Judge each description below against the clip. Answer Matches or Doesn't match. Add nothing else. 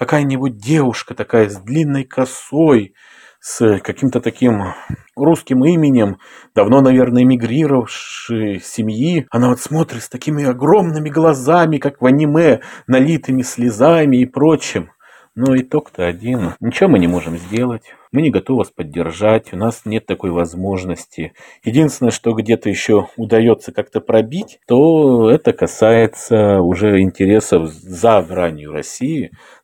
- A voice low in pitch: Matches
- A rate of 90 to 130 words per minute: Matches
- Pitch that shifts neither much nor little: Matches